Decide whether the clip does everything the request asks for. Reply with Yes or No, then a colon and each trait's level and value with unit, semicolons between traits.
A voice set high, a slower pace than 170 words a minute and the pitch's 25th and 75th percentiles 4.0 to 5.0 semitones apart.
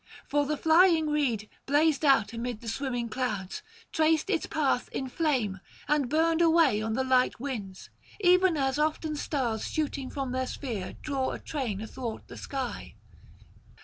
Yes: very high, 270 Hz; average, 155 wpm; average, 4.6 semitones